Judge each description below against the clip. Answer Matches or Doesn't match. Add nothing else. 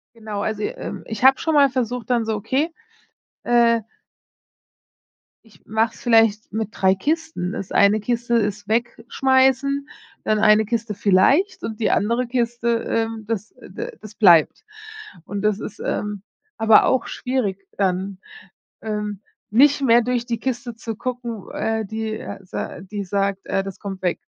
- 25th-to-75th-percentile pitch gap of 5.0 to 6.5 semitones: Doesn't match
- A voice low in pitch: Doesn't match